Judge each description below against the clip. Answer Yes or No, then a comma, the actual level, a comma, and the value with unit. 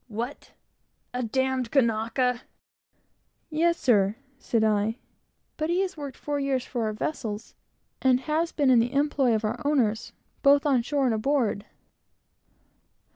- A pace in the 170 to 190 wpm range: No, average, 145 wpm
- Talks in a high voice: Yes, very high, 255 Hz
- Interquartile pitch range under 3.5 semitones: No, average, 4.2 semitones